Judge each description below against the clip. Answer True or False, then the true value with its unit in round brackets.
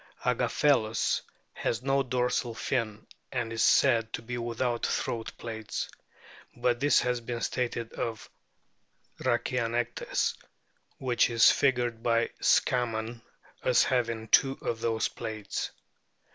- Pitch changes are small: True (1.6 semitones)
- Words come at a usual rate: False (115 wpm)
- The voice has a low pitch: True (120 Hz)